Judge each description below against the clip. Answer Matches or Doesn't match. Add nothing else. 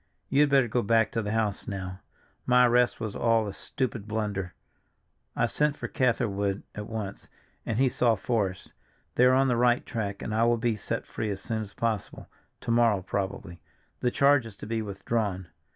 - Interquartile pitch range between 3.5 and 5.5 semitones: Doesn't match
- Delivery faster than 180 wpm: Matches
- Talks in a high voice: Doesn't match